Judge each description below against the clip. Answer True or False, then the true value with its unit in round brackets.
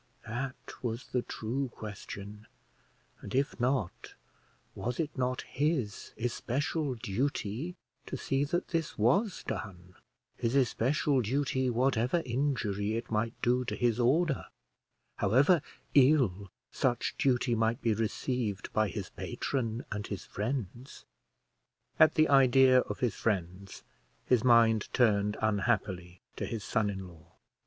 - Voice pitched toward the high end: False (120 Hz)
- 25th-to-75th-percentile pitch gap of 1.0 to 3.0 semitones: False (4.1 semitones)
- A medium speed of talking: False (130 wpm)